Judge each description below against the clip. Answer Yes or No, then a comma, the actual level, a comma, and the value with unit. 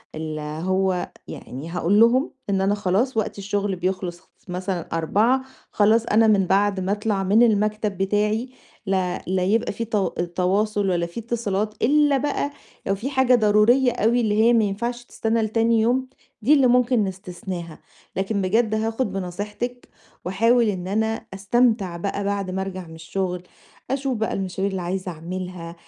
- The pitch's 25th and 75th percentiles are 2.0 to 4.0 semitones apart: Yes, average, 3.5 semitones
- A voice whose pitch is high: Yes, high, 205 Hz